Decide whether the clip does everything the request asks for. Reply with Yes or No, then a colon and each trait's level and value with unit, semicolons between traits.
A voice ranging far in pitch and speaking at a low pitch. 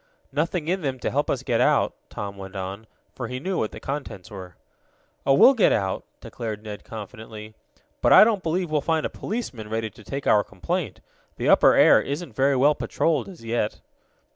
Yes: wide, 6.6 semitones; low, 125 Hz